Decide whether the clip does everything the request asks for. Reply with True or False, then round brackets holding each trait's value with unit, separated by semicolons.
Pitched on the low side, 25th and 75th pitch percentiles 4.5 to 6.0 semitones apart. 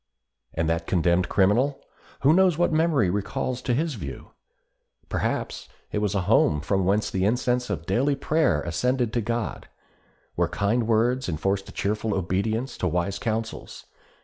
True (110 Hz; 5.1 semitones)